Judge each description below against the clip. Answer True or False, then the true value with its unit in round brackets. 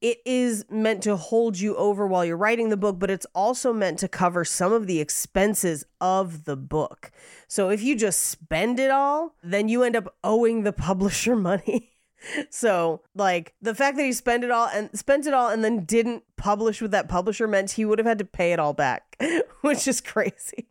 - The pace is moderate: False (210 wpm)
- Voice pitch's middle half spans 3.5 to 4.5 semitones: True (3.8 semitones)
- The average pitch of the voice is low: False (215 Hz)